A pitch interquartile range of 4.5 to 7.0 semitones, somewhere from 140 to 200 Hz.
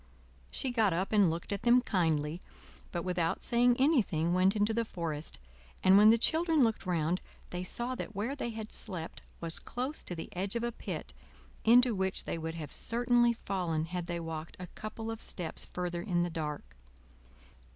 Yes: wide, 5.6 semitones; high, 190 Hz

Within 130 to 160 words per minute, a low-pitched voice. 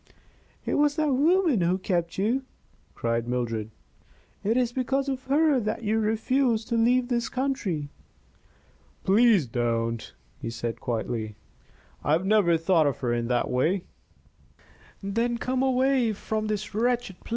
No: average, 150 wpm; high, 215 Hz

